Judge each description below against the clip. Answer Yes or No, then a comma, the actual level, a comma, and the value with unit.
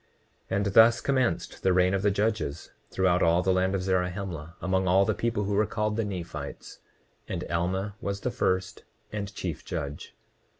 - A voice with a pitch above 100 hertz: No, very low, 95 Hz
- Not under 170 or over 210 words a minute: Yes, average, 180 wpm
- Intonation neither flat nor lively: No, narrow, 2.3 semitones